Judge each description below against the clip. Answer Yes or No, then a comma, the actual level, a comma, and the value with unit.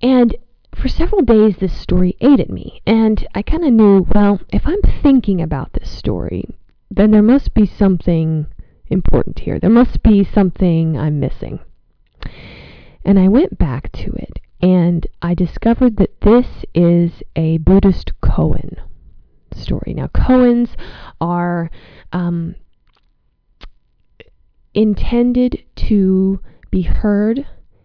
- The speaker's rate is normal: No, slow, 125 wpm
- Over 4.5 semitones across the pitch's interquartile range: Yes, average, 5.1 semitones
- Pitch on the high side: Yes, high, 195 Hz